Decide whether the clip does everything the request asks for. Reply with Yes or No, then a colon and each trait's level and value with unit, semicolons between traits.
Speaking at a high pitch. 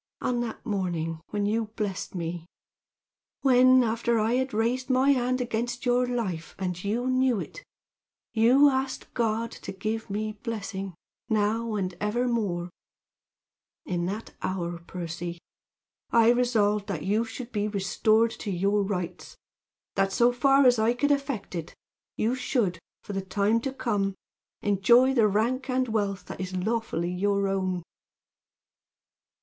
Yes: high, 220 Hz